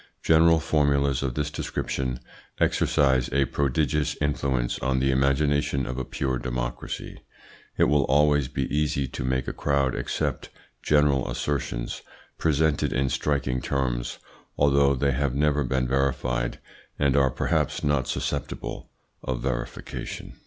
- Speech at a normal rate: No, slow, 130 wpm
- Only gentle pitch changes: Yes, narrow, 2.0 semitones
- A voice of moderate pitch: No, very low, 70 Hz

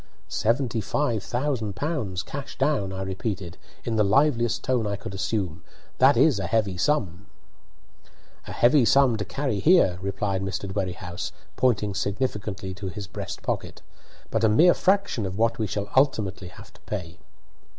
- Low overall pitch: Yes, low, 105 Hz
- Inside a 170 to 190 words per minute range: No, average, 155 wpm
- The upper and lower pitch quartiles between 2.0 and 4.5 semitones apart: No, average, 5.0 semitones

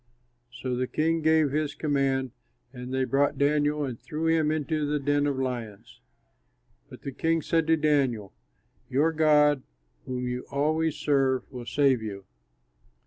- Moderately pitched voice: Yes, medium, 145 Hz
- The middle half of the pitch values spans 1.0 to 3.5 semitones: Yes, average, 2.9 semitones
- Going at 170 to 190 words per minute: No, average, 150 wpm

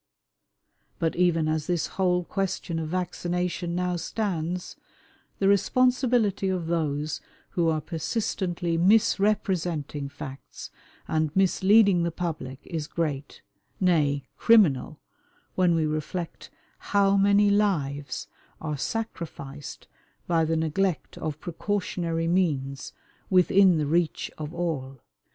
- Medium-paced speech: No, slow, 110 wpm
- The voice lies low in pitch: No, medium, 170 Hz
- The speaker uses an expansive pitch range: No, average, 3.6 semitones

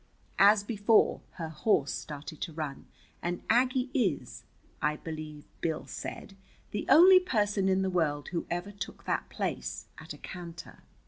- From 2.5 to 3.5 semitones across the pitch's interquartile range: No, average, 5.0 semitones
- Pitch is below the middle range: No, medium, 185 Hz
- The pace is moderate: Yes, average, 150 wpm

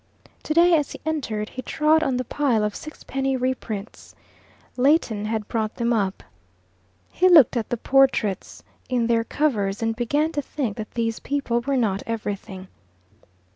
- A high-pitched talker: Yes, high, 240 Hz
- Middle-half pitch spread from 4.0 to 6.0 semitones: Yes, average, 4.7 semitones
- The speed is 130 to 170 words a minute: Yes, average, 155 wpm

